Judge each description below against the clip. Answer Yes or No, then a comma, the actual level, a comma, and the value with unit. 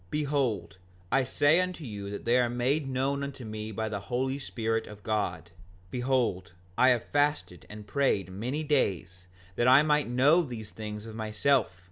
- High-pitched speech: No, low, 120 Hz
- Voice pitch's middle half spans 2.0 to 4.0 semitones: No, average, 4.8 semitones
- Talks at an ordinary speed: Yes, average, 170 wpm